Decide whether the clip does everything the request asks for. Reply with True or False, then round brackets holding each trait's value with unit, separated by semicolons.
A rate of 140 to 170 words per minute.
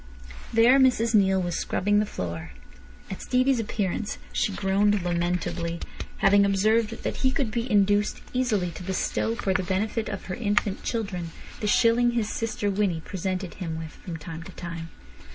True (165 wpm)